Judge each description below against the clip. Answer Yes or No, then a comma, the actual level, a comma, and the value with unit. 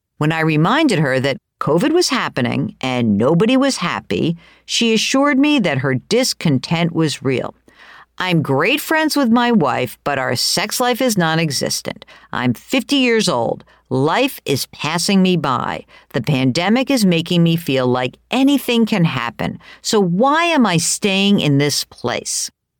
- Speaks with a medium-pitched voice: Yes, medium, 175 Hz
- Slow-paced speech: No, average, 155 wpm